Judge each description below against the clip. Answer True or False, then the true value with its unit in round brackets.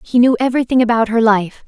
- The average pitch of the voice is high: True (235 Hz)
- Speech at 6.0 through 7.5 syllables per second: True (6.5 syllables/s)